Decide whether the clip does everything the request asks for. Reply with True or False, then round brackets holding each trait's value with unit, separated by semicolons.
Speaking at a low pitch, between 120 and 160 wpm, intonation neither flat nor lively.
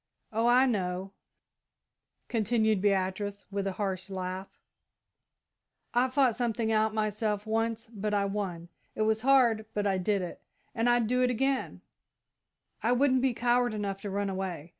False (215 Hz; 155 wpm; 3.4 semitones)